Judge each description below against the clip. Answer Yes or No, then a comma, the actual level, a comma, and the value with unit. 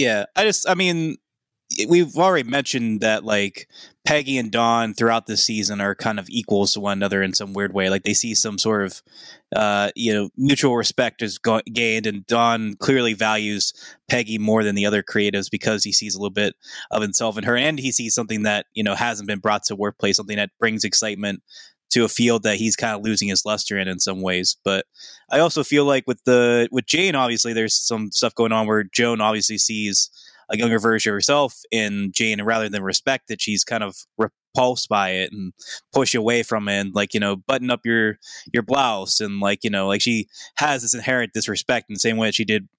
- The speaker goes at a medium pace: No, fast, 225 wpm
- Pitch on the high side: No, low, 110 Hz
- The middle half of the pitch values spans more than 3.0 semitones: No, narrow, 2.5 semitones